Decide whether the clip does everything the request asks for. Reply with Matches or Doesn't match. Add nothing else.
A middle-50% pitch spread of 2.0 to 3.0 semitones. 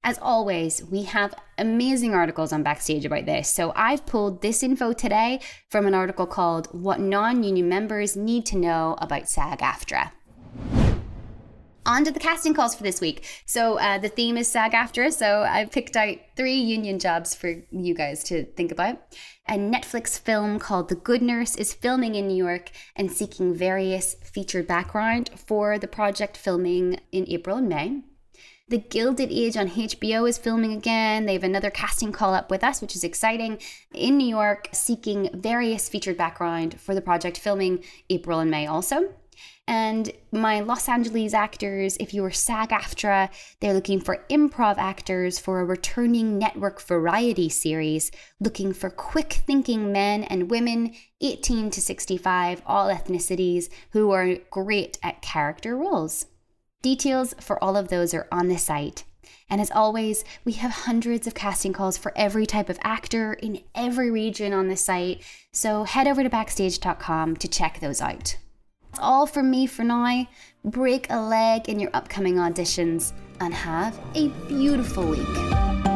Doesn't match